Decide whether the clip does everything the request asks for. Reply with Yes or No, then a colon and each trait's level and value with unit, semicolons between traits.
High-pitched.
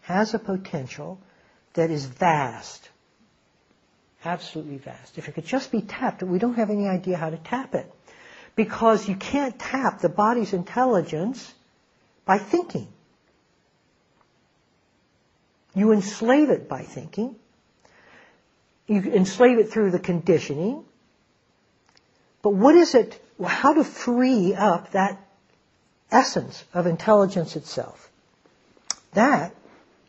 Yes: high, 205 Hz